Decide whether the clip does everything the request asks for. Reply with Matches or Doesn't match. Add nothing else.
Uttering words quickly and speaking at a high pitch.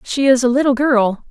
Matches